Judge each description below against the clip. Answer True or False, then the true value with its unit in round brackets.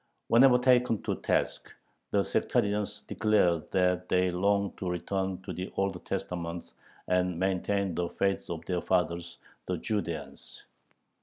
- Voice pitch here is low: True (95 Hz)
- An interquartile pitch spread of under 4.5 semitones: True (2.4 semitones)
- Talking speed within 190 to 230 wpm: False (135 wpm)